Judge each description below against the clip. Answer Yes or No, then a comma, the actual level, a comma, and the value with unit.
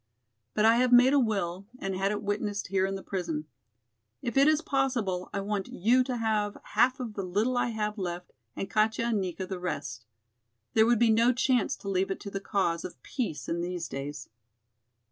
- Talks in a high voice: Yes, high, 205 Hz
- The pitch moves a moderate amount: Yes, average, 4.3 semitones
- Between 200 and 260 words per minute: Yes, fast, 205 wpm